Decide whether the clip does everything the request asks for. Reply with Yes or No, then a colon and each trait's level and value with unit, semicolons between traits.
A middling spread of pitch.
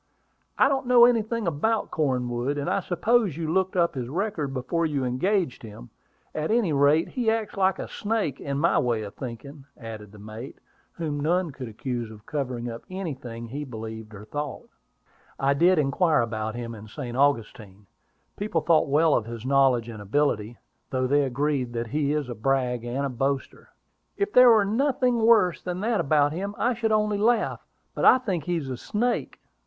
No: wide, 7.6 semitones